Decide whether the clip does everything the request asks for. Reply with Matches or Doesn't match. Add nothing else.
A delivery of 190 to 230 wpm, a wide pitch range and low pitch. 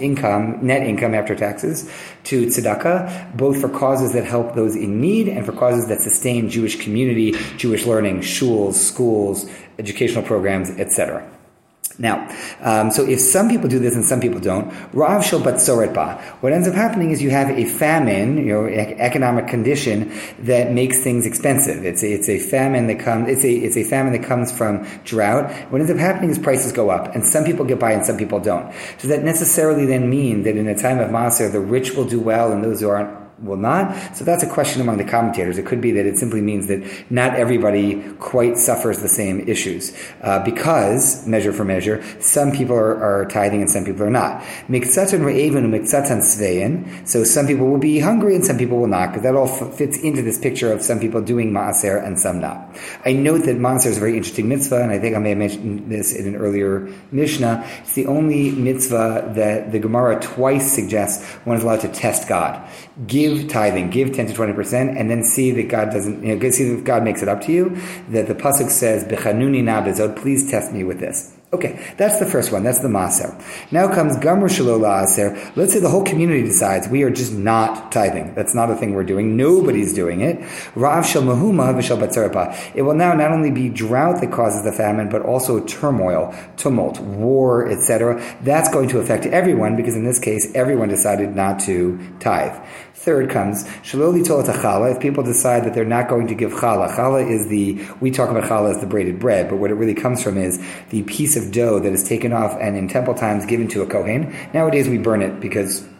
Doesn't match